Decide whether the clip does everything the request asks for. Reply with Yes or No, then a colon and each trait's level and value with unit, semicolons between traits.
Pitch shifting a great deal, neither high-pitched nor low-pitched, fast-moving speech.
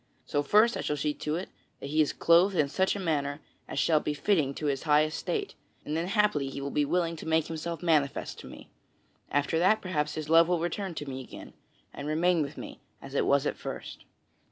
No: average, 3.2 semitones; medium, 155 Hz; fast, 225 wpm